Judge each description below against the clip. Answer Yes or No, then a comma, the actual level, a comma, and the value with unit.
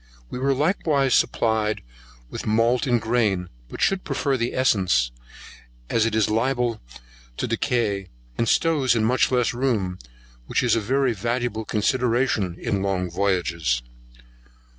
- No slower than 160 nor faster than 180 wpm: No, average, 140 wpm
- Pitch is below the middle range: Yes, low, 115 Hz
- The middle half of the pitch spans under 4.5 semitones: Yes, average, 4.1 semitones